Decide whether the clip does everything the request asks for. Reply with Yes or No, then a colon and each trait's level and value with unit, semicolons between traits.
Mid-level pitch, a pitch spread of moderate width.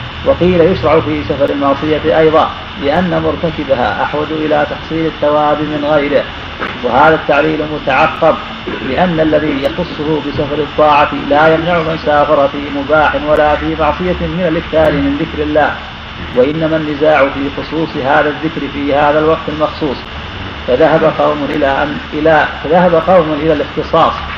No: medium, 150 Hz; narrow, 1.5 semitones